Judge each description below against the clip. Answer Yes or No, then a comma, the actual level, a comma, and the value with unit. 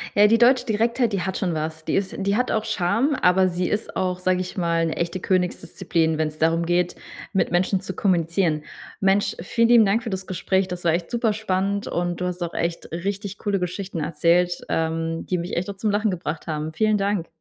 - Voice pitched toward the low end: No, medium, 185 Hz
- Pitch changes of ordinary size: Yes, average, 3.2 semitones